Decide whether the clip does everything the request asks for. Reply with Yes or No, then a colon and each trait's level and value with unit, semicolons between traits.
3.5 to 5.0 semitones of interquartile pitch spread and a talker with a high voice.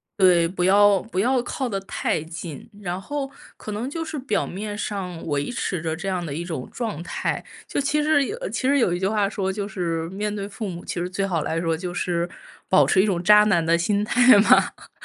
Yes: average, 3.8 semitones; high, 195 Hz